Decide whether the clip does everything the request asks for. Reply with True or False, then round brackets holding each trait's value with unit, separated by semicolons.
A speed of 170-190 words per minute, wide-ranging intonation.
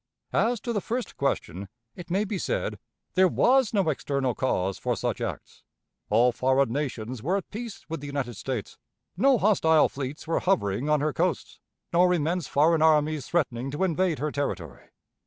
True (175 wpm; 6.1 semitones)